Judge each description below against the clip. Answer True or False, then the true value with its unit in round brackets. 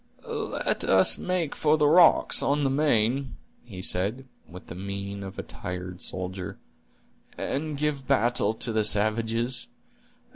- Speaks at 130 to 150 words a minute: True (140 wpm)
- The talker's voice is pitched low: True (115 Hz)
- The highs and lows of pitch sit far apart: True (6.2 semitones)